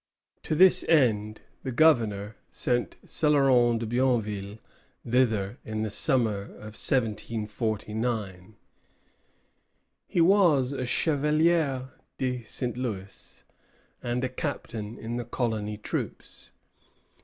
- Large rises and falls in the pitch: No, average, 3.7 semitones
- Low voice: Yes, low, 120 Hz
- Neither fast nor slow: No, slow, 100 wpm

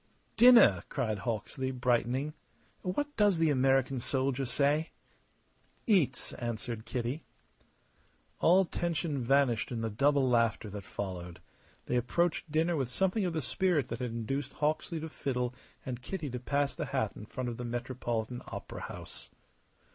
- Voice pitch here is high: No, low, 130 Hz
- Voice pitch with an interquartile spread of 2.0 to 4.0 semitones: No, average, 4.5 semitones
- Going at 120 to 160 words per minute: Yes, average, 145 wpm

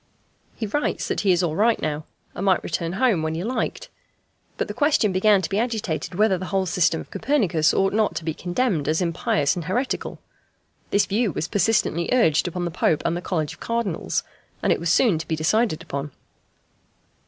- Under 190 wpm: No, average, 200 wpm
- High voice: No, medium, 180 Hz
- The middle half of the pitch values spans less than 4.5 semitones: No, average, 4.9 semitones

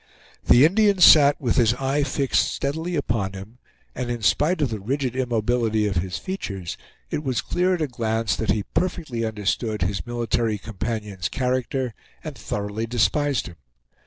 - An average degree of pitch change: Yes, average, 4.8 semitones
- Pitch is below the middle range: Yes, low, 120 Hz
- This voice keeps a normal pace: Yes, average, 160 wpm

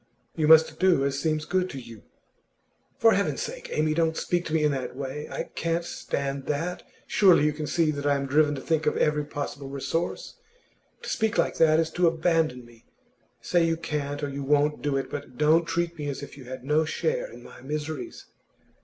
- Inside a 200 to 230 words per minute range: Yes, fast, 205 wpm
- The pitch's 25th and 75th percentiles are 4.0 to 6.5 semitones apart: No, average, 2.8 semitones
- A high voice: No, medium, 150 Hz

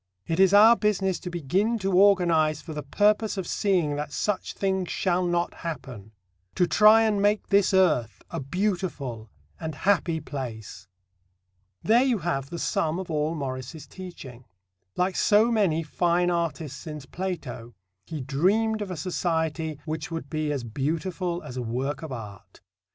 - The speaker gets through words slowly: No, average, 160 wpm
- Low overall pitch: No, medium, 170 Hz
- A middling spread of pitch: Yes, average, 4.8 semitones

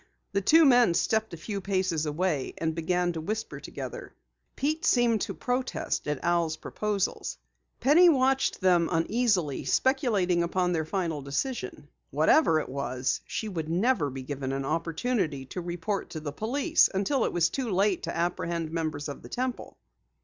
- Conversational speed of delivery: Yes, average, 165 wpm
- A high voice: No, medium, 180 Hz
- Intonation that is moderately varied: No, wide, 6.7 semitones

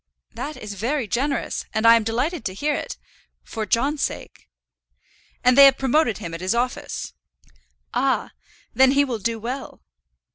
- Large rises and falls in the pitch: No, average, 3.8 semitones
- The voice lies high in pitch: Yes, high, 245 Hz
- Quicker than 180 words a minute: No, average, 160 wpm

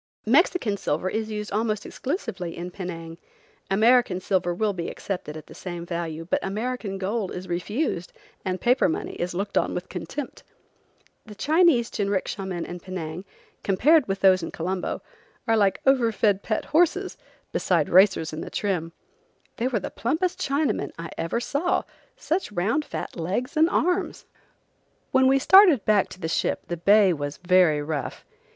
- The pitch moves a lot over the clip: Yes, wide, 5.8 semitones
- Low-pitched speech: No, high, 195 Hz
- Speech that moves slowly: No, average, 160 wpm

